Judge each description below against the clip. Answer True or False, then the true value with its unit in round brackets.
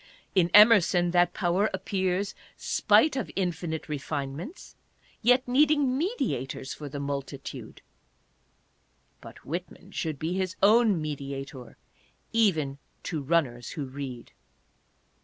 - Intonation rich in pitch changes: True (6.3 semitones)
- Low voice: False (170 Hz)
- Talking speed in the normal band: False (105 wpm)